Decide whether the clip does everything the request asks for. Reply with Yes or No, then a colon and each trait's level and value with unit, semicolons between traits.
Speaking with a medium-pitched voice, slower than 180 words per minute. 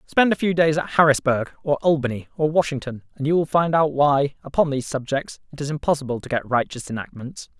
No: medium, 145 Hz; fast, 205 wpm